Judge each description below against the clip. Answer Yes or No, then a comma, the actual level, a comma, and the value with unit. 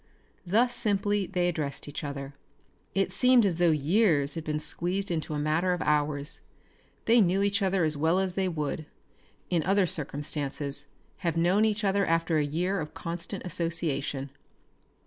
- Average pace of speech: Yes, average, 165 wpm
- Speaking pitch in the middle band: Yes, medium, 170 Hz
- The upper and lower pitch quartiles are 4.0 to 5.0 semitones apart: Yes, average, 4.4 semitones